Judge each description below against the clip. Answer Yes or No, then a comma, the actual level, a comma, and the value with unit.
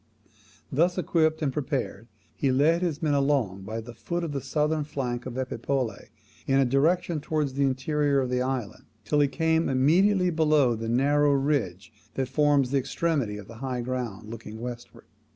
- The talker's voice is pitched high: No, low, 135 Hz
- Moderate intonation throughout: Yes, average, 3.8 semitones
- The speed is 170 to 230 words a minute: Yes, average, 175 wpm